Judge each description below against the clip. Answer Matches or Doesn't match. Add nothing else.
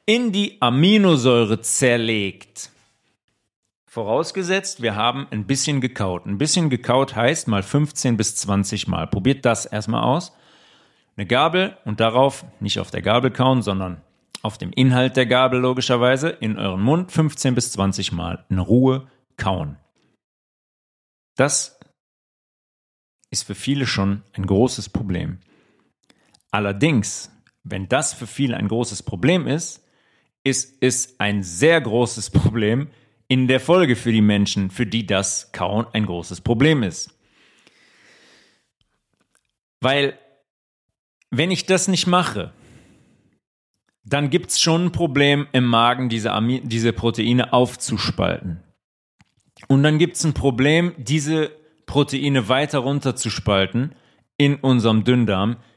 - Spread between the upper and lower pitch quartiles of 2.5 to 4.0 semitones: Doesn't match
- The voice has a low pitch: Matches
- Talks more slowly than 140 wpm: Matches